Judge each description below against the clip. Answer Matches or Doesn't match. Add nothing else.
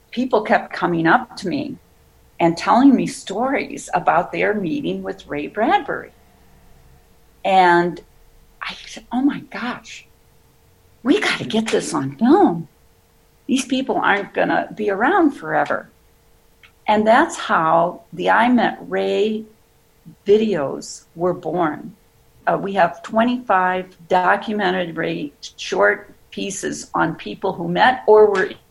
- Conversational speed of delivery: Doesn't match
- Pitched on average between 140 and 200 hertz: Matches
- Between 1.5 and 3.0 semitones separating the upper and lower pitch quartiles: Doesn't match